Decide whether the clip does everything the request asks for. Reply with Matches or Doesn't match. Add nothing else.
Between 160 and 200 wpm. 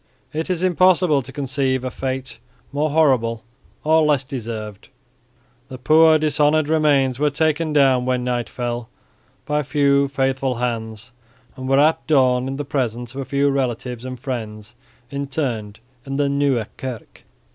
Doesn't match